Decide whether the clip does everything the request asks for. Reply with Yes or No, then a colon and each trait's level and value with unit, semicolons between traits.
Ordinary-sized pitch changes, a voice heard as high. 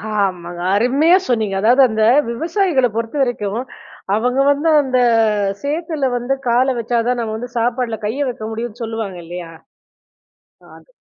Yes: average, 3.7 semitones; high, 240 Hz